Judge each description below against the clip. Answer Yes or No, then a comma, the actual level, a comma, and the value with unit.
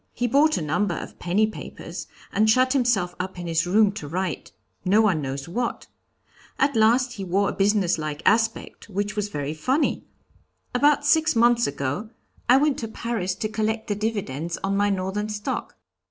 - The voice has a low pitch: No, high, 205 Hz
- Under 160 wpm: No, average, 180 wpm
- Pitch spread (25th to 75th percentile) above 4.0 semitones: Yes, average, 4.7 semitones